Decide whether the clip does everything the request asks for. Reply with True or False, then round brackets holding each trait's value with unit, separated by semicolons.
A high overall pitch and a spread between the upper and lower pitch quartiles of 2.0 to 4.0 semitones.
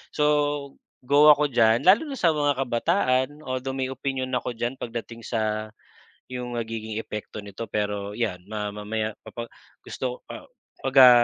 False (120 Hz; 3.6 semitones)